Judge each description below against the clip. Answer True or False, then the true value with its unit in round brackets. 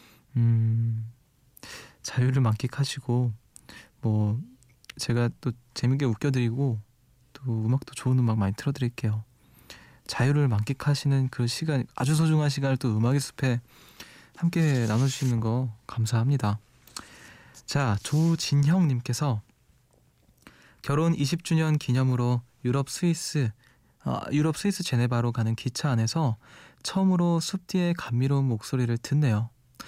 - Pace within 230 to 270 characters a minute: True (260 characters per minute)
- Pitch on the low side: True (130 Hz)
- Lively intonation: False (3.2 semitones)